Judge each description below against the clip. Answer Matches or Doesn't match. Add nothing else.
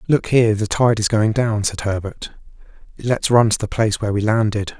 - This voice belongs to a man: Matches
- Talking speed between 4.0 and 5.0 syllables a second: Doesn't match